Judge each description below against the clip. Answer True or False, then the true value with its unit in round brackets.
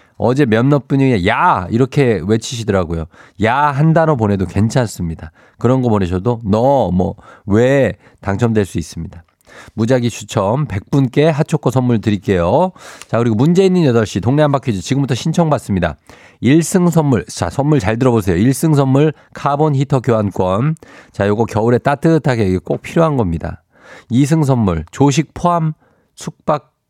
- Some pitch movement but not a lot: False (5.9 semitones)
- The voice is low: True (120 Hz)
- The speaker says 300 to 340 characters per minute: True (305 characters per minute)